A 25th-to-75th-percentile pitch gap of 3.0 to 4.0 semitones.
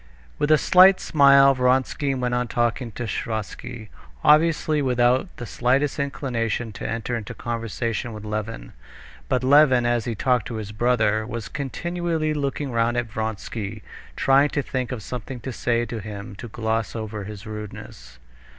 Yes: average, 3.5 semitones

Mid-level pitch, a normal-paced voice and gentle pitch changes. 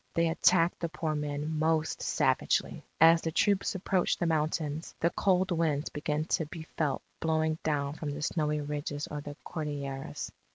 Yes: medium, 155 Hz; average, 165 wpm; narrow, 2.0 semitones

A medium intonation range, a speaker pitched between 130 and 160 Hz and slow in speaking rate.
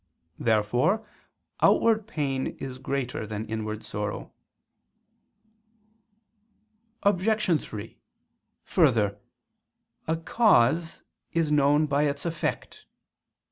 No: wide, 7.1 semitones; medium, 140 Hz; slow, 80 wpm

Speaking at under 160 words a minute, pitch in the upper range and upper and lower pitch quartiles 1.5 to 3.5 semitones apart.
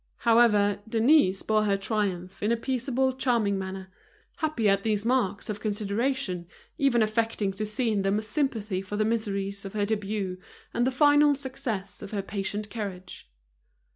No: average, 165 wpm; high, 215 Hz; average, 3.2 semitones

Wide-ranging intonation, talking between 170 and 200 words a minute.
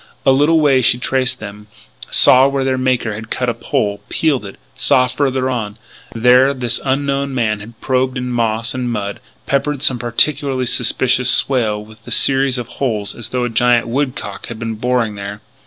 No: average, 2.7 semitones; average, 185 wpm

